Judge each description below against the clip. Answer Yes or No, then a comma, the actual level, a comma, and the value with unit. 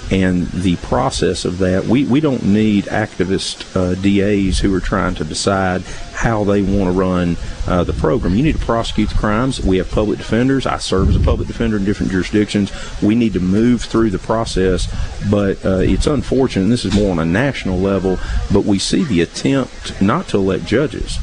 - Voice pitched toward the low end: Yes, very low, 95 Hz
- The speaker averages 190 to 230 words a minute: Yes, fast, 205 wpm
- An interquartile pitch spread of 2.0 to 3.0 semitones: Yes, narrow, 2.4 semitones